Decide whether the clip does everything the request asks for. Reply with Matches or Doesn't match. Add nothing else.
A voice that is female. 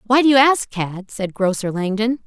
Matches